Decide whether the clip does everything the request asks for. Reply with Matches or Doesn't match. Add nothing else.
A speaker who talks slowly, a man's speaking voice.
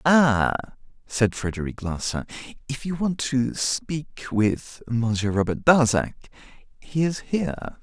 Matches